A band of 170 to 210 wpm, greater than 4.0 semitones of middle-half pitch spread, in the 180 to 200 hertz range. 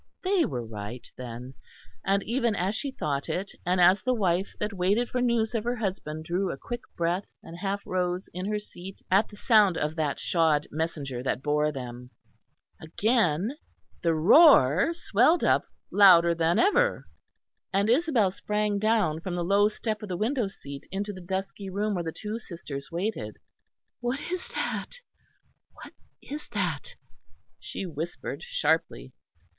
No: average, 160 wpm; average, 5.2 semitones; high, 190 Hz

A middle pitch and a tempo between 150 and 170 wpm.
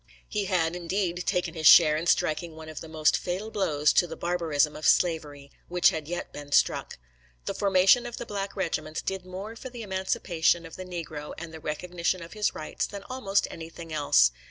No: medium, 170 Hz; average, 200 wpm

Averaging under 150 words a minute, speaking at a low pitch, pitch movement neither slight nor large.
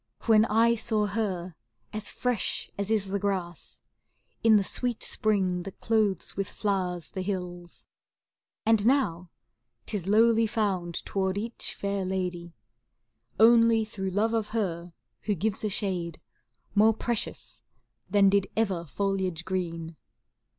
No: slow, 135 wpm; high, 200 Hz; average, 3.3 semitones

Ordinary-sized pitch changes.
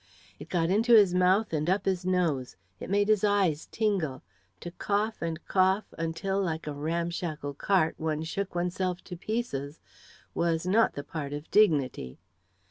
Yes: average, 3.9 semitones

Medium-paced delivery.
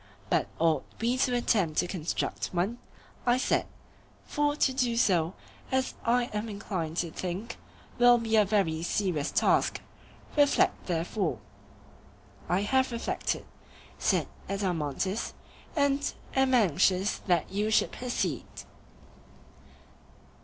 No: slow, 115 wpm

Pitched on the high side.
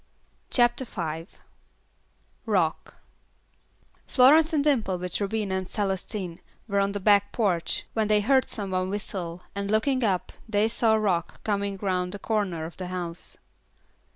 Yes: high, 200 Hz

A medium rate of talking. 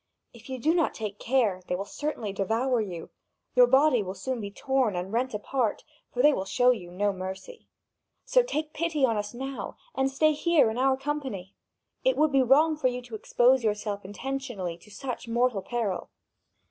Yes: average, 190 wpm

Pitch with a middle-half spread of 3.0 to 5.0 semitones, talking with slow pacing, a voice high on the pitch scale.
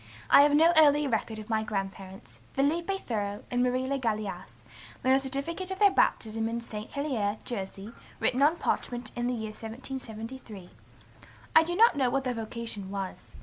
No: average, 4.5 semitones; average, 175 wpm; high, 240 Hz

